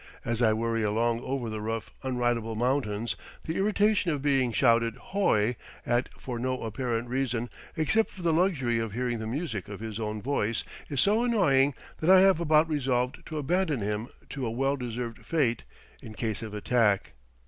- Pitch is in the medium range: No, low, 125 Hz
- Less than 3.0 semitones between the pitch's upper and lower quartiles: No, average, 4.4 semitones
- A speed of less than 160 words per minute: No, average, 180 wpm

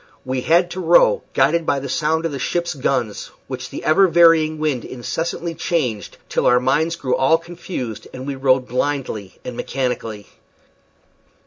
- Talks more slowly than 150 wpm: No, average, 160 wpm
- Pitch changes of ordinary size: Yes, average, 4.7 semitones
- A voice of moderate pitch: Yes, medium, 145 Hz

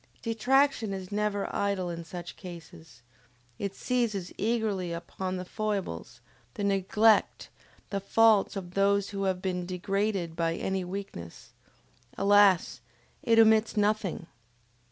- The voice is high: Yes, high, 195 Hz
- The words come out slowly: Yes, slow, 120 wpm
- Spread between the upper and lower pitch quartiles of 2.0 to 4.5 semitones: Yes, average, 2.8 semitones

